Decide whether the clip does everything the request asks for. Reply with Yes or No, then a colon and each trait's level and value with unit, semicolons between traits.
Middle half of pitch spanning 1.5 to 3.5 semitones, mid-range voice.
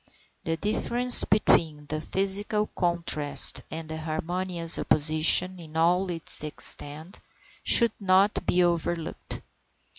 Yes: average, 3.2 semitones; medium, 170 Hz